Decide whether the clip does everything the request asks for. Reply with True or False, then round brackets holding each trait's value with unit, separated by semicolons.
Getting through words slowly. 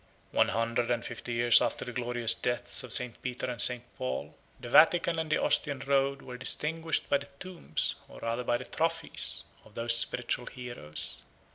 False (180 wpm)